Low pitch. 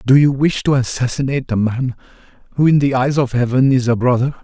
Yes: low, 130 Hz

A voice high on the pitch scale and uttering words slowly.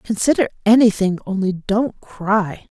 Yes: high, 205 Hz; slow, 105 wpm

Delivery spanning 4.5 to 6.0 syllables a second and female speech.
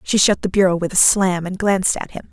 Yes: 5.9 syllables/s; female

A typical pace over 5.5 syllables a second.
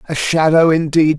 No: 5.0 syllables/s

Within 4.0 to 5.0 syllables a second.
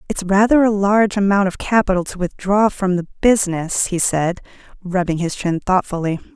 No: 5.3 syllables/s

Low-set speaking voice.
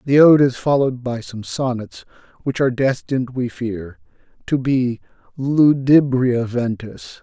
Yes: low, 125 Hz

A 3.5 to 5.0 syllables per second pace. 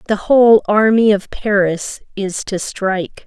Yes: 4.1 syllables/s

